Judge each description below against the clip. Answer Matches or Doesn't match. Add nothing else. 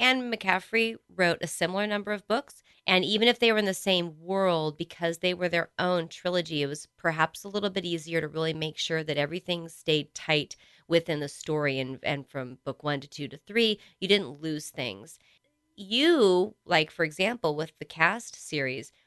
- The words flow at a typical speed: Matches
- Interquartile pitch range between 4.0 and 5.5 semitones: Matches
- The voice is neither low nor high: Matches